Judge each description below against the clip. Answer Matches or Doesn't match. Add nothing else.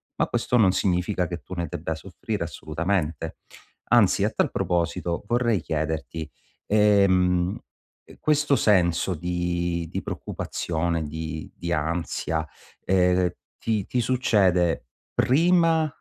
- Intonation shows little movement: Doesn't match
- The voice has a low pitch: Matches